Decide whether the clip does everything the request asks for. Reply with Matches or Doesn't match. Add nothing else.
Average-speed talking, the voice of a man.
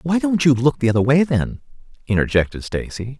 Matches